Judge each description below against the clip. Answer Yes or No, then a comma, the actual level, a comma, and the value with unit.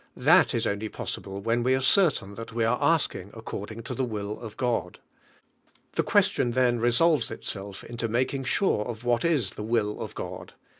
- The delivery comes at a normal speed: Yes, average, 185 wpm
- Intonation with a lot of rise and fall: No, average, 2.9 semitones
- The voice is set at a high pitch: No, low, 115 Hz